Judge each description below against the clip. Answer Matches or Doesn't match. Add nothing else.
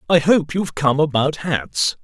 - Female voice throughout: Doesn't match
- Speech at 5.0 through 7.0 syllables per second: Doesn't match